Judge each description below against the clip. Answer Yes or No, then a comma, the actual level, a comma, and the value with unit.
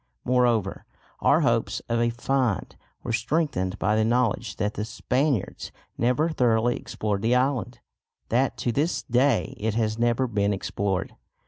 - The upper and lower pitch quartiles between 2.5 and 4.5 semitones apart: Yes, average, 2.9 semitones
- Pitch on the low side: Yes, low, 115 Hz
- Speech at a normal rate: Yes, average, 145 wpm